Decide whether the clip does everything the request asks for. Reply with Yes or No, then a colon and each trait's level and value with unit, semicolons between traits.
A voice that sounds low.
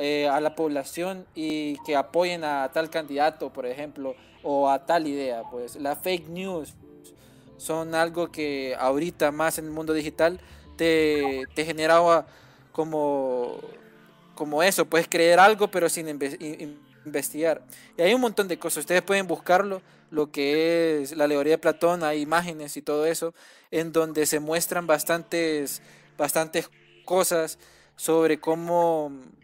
No: medium, 155 Hz